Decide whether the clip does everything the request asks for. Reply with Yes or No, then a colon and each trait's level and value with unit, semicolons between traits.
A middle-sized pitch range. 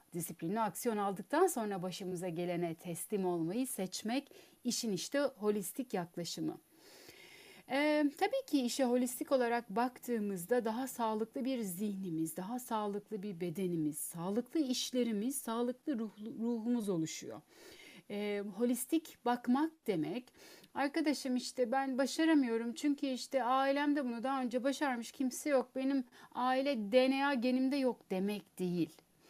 Yes: average, 4.9 semitones